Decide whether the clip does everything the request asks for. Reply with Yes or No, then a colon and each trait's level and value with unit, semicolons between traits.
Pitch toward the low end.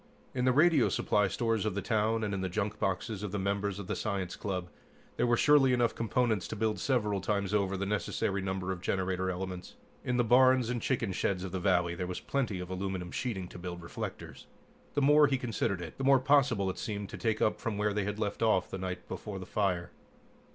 Yes: low, 100 Hz